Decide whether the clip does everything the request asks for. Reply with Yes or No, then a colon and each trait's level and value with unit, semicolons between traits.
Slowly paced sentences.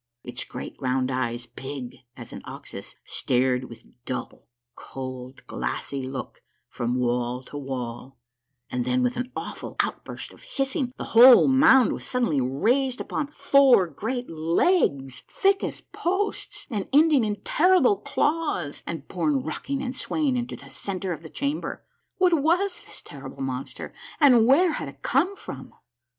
No: average, 155 wpm